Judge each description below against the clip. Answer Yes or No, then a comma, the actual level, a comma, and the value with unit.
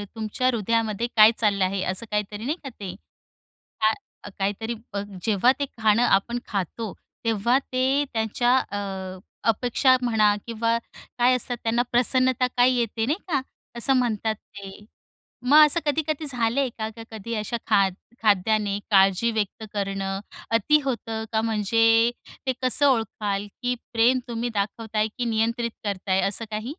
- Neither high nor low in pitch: No, high, 225 Hz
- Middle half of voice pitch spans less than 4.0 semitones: Yes, average, 3.1 semitones